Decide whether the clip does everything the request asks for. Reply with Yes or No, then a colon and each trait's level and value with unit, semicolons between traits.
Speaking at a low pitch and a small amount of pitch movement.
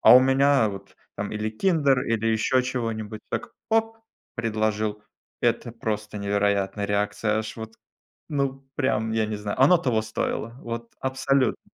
No: low, 110 Hz; average, 3.6 semitones